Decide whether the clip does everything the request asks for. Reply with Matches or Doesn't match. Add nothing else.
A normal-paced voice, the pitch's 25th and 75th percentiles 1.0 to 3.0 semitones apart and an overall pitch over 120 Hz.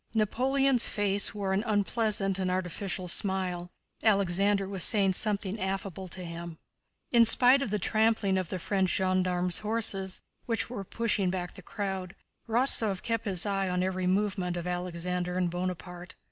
Matches